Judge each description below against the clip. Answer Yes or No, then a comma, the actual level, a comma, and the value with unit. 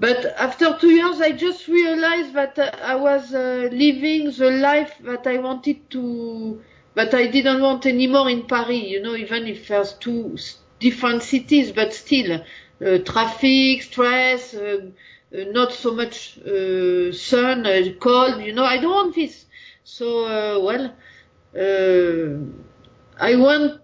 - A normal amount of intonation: Yes, average, 4.2 semitones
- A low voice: No, very high, 250 Hz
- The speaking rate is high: No, average, 150 wpm